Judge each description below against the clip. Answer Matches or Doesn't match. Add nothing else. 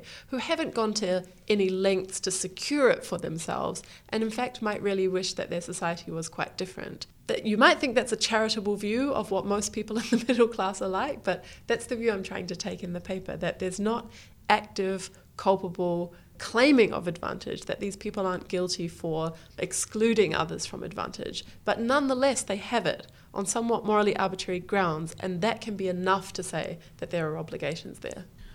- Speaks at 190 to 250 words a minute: Matches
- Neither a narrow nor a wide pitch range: Matches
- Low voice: Doesn't match